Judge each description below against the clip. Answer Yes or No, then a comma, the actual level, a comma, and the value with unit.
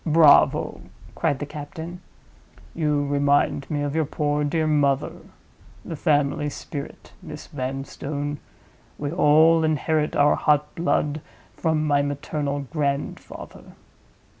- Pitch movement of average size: No, narrow, 1.5 semitones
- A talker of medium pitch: Yes, medium, 150 Hz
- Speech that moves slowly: Yes, slow, 115 wpm